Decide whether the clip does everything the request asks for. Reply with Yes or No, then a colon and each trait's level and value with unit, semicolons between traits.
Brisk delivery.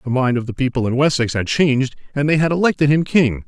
Yes: fast, 260 wpm